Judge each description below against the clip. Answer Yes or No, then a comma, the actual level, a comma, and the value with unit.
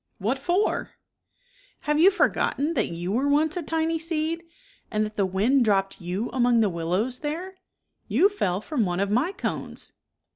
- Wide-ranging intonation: Yes, wide, 8.4 semitones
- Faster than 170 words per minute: Yes, average, 185 wpm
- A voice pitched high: Yes, very high, 265 Hz